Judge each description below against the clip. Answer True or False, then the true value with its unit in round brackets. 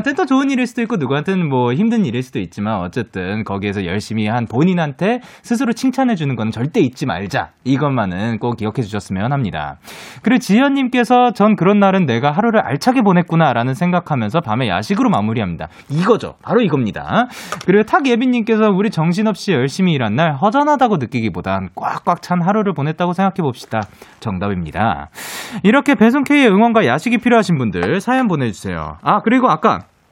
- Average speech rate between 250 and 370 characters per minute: False (415 characters per minute)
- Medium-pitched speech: True (175 Hz)